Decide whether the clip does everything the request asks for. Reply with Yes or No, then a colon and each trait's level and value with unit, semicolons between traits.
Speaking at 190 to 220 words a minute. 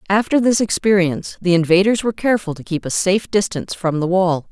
Yes: average, 200 wpm